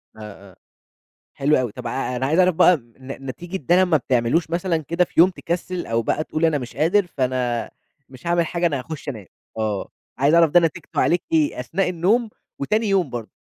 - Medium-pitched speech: Yes, medium, 155 Hz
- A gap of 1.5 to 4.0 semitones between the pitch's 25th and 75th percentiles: No, wide, 5.5 semitones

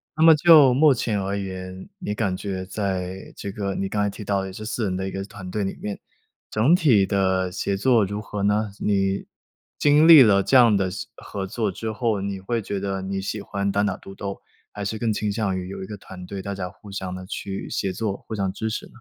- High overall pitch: No, low, 100 Hz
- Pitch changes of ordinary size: No, narrow, 2.1 semitones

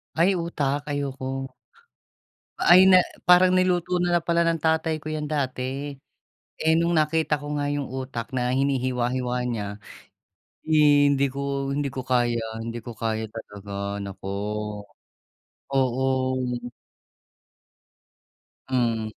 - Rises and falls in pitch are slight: No, average, 4.3 semitones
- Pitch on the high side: No, medium, 140 Hz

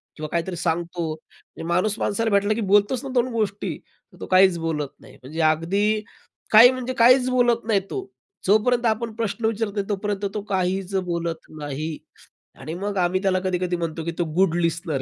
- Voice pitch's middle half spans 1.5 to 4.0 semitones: No, average, 4.5 semitones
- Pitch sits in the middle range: No, high, 195 Hz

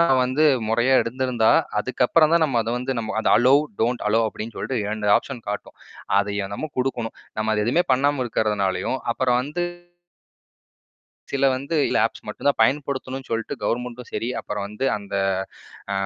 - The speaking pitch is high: No, low, 125 Hz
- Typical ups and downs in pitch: Yes, average, 3.3 semitones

